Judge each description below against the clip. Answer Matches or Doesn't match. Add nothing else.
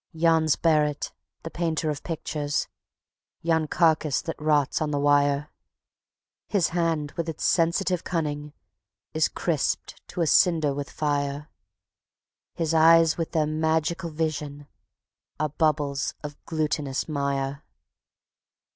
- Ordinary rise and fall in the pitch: Doesn't match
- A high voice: Doesn't match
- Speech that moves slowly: Matches